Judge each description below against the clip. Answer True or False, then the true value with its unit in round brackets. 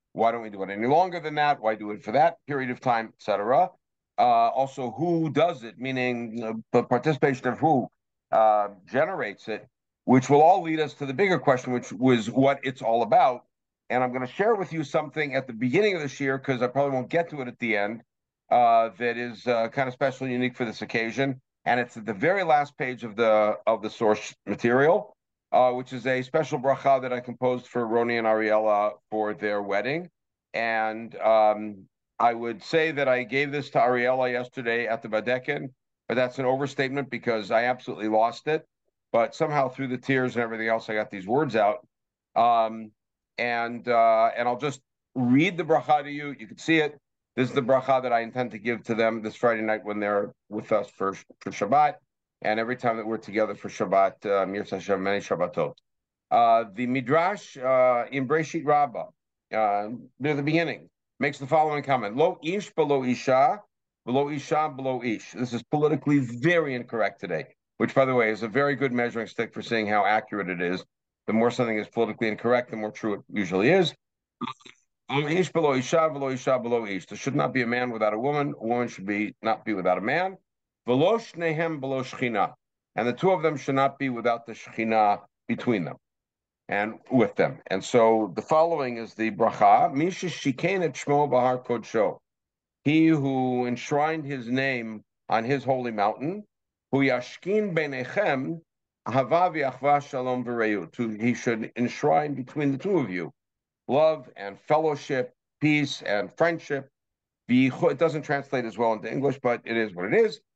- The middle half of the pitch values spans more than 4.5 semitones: False (4.2 semitones)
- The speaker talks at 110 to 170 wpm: False (180 wpm)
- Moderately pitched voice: False (125 Hz)